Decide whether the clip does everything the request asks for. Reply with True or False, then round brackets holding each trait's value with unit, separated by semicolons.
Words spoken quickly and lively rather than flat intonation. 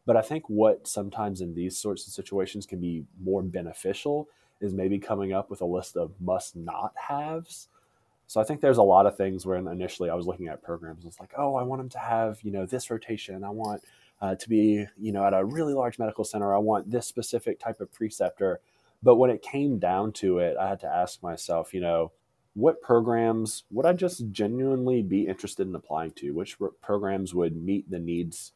False (215 wpm; 4.2 semitones)